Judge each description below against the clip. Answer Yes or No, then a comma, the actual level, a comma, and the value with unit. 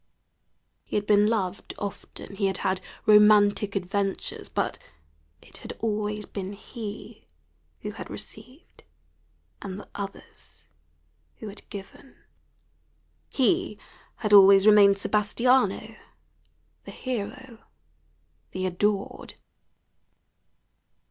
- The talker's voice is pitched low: No, high, 205 Hz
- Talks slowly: Yes, slow, 95 wpm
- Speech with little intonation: Yes, narrow, 1.5 semitones